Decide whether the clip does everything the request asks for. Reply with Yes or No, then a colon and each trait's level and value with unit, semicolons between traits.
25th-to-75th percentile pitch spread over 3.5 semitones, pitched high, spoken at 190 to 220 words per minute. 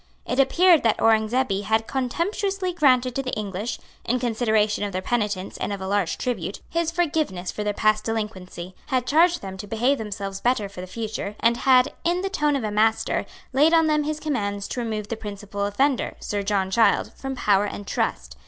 Yes: average, 5.0 semitones; high, 225 Hz; average, 200 wpm